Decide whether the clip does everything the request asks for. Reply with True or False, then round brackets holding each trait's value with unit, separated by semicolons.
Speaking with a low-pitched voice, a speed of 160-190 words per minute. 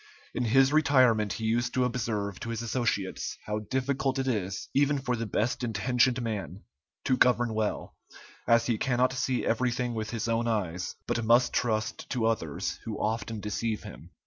True (115 Hz; 170 wpm)